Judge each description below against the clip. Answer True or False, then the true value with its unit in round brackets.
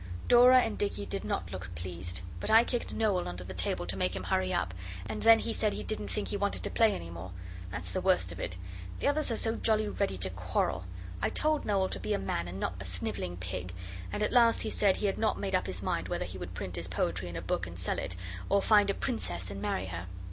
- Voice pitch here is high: False (95 Hz)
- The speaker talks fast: True (260 wpm)